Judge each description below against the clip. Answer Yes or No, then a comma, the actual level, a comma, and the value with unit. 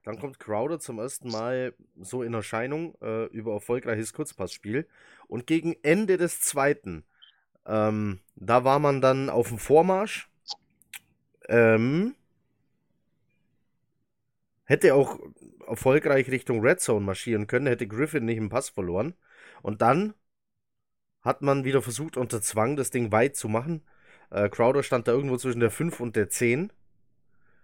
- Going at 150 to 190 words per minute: No, average, 140 wpm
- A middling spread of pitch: Yes, average, 4.1 semitones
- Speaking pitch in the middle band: No, low, 120 Hz